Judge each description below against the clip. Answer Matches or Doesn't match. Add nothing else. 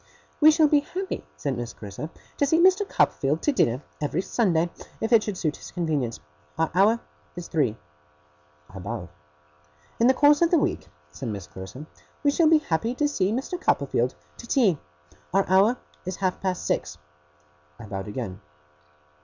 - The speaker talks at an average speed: Matches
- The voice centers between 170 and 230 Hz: Matches